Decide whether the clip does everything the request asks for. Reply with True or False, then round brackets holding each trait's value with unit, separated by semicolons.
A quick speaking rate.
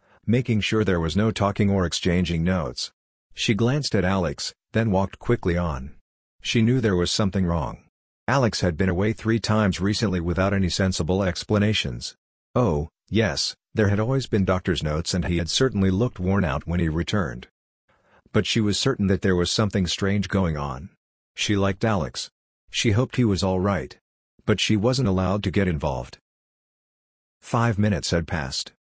False (170 wpm)